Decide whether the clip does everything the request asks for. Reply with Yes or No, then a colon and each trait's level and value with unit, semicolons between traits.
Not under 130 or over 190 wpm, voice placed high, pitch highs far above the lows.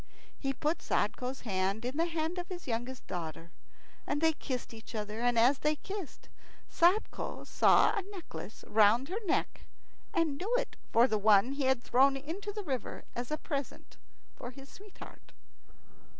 Yes: average, 165 wpm; very high, 270 Hz; wide, 6.1 semitones